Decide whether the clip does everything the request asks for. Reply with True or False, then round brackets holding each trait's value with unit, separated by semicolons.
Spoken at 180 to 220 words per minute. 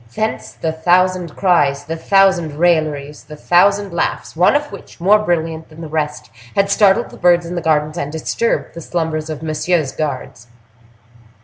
False (170 wpm)